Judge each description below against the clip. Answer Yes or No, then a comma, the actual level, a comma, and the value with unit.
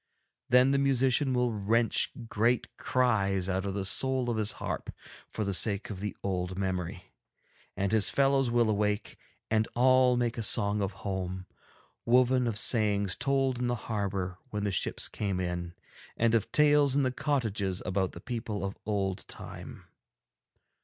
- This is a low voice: Yes, low, 110 Hz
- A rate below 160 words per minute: No, average, 165 wpm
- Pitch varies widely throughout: No, average, 4.2 semitones